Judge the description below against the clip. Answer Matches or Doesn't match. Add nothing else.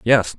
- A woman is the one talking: Doesn't match